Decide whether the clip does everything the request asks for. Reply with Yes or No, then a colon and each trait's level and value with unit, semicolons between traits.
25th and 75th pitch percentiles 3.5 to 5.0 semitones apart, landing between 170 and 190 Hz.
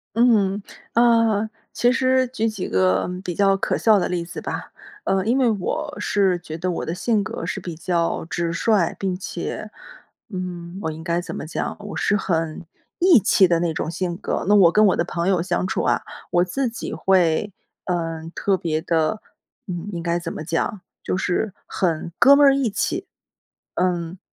Yes: average, 4.0 semitones; medium, 185 Hz